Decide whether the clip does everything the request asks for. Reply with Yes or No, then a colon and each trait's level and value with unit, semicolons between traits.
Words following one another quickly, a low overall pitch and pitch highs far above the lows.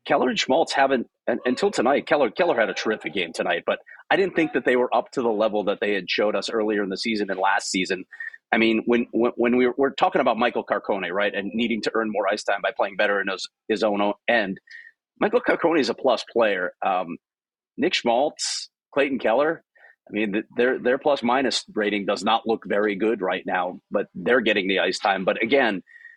Yes: fast, 220 wpm; low, 120 Hz; wide, 7.4 semitones